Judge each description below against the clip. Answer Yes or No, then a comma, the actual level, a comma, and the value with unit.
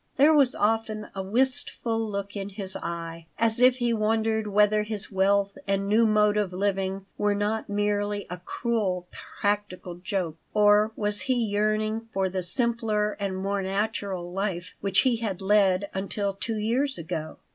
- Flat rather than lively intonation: Yes, narrow, 2.3 semitones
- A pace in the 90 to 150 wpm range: No, average, 160 wpm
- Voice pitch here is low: No, high, 205 Hz